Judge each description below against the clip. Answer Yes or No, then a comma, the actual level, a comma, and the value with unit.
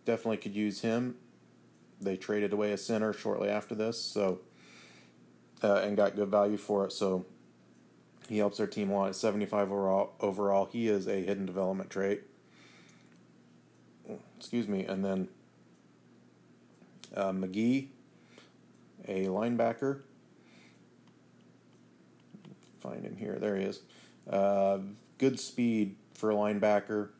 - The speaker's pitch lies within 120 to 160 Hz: No, low, 100 Hz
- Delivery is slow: Yes, slow, 125 wpm